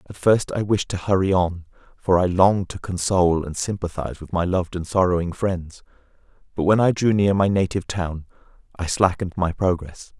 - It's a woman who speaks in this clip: No, male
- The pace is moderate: Yes, average, 190 wpm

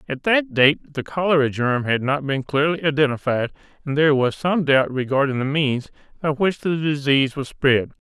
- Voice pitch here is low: No, medium, 145 Hz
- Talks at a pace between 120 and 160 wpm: No, average, 185 wpm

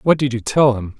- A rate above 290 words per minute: Yes, fast, 300 wpm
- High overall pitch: No, low, 125 Hz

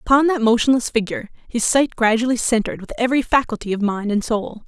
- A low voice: No, high, 230 Hz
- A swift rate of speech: No, average, 195 wpm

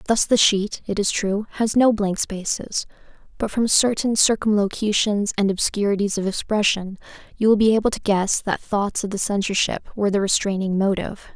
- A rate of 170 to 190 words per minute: Yes, average, 175 wpm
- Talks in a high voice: Yes, high, 205 Hz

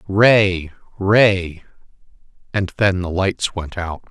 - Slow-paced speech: Yes, slow, 115 wpm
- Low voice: Yes, very low, 95 Hz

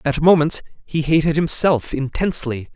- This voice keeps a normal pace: No, slow, 130 wpm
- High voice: No, medium, 155 Hz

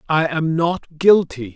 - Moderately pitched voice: Yes, medium, 160 Hz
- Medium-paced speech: Yes, average, 155 wpm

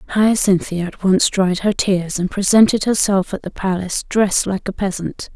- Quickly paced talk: No, average, 180 wpm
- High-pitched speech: Yes, high, 195 Hz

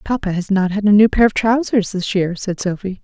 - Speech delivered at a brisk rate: Yes, fast, 255 wpm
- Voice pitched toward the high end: Yes, high, 200 Hz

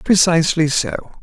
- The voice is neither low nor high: Yes, medium, 155 Hz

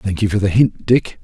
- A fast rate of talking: Yes, fast, 290 wpm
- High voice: No, low, 100 Hz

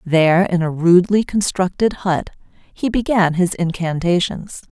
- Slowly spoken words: Yes, slow, 125 wpm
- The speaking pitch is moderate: Yes, medium, 180 Hz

